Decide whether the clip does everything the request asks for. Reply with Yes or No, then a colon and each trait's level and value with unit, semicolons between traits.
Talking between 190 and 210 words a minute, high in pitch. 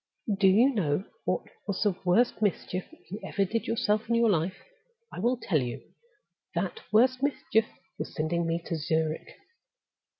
No: average, 160 wpm; high, 195 Hz